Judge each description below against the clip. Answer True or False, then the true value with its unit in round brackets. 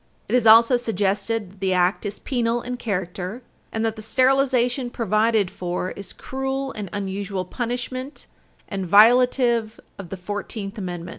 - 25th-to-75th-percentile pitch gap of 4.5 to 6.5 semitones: False (3.9 semitones)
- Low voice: False (220 Hz)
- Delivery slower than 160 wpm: True (150 wpm)